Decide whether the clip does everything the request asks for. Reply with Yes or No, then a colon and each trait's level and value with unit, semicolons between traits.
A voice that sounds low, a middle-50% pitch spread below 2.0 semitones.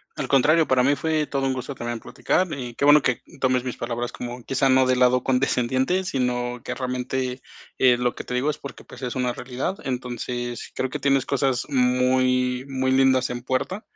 Yes: low, 130 Hz; narrow, 1.4 semitones